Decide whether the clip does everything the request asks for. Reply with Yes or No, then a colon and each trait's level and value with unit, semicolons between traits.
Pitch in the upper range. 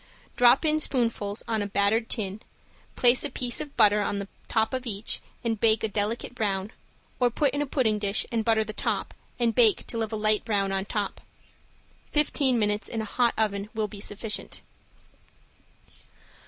Yes: high, 220 Hz